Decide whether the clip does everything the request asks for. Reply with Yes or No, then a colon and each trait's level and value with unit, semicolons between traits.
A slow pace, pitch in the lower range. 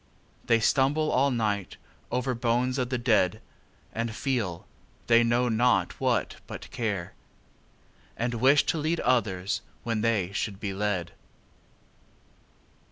Yes: slow, 120 wpm; low, 115 Hz